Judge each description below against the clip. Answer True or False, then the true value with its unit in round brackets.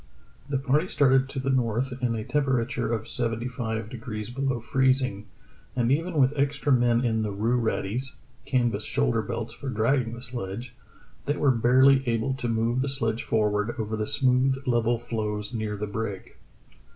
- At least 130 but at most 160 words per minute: False (170 wpm)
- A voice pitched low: True (120 Hz)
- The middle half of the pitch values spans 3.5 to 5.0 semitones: False (2.9 semitones)